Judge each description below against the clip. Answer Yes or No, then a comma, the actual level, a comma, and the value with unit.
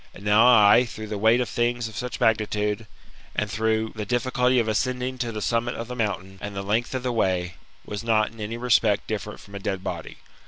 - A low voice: Yes, low, 110 Hz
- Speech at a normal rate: No, fast, 225 wpm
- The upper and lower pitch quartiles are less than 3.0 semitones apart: Yes, narrow, 2.5 semitones